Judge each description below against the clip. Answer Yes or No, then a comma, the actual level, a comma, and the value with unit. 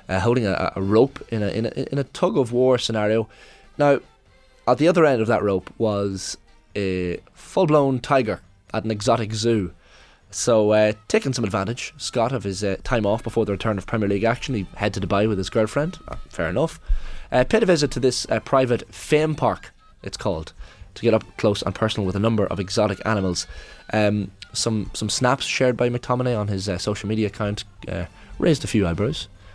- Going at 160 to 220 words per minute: Yes, fast, 205 wpm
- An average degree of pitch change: Yes, average, 4.0 semitones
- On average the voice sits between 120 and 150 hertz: No, low, 110 Hz